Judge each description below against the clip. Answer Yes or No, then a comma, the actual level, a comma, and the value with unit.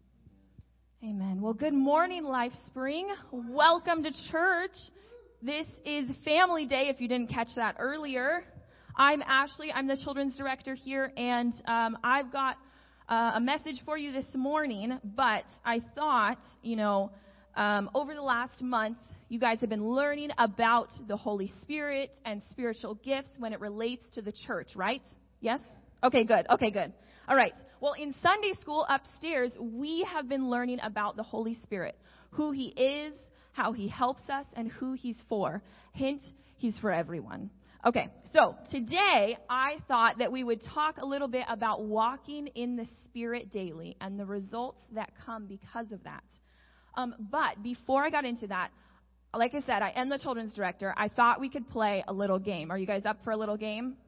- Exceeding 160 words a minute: Yes, average, 175 wpm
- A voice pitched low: No, high, 245 Hz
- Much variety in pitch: No, average, 4.2 semitones